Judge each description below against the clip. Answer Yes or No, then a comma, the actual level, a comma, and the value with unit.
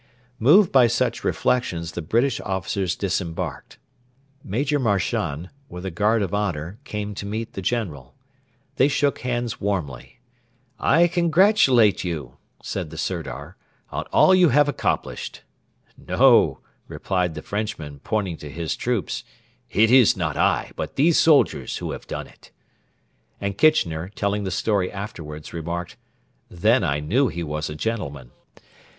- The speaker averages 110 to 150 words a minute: Yes, average, 140 wpm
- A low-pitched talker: Yes, low, 100 Hz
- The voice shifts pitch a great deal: Yes, wide, 6.5 semitones